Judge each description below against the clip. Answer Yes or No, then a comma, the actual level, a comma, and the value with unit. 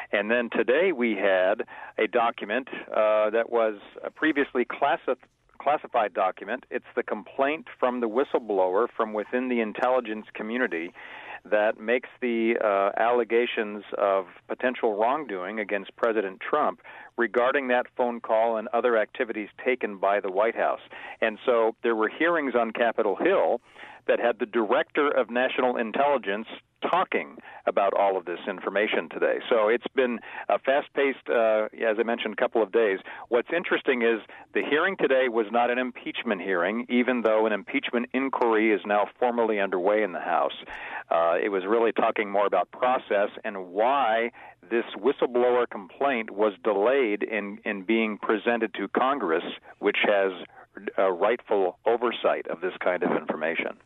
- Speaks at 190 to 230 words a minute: No, average, 155 wpm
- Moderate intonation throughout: No, narrow, 2.3 semitones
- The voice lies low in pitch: Yes, low, 115 Hz